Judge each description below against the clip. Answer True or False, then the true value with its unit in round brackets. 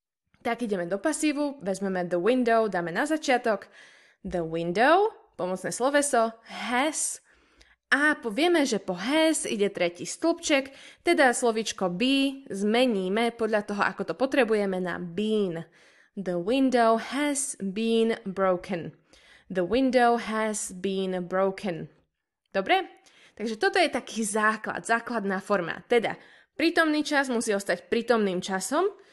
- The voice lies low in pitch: False (225 Hz)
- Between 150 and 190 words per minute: False (120 wpm)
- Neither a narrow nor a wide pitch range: False (6.1 semitones)